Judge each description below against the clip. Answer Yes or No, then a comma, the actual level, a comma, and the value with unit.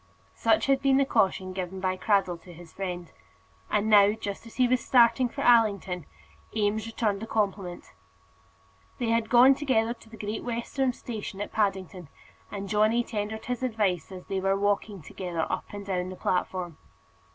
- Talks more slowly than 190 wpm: Yes, average, 175 wpm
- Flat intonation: No, average, 3.6 semitones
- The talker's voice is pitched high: Yes, high, 205 Hz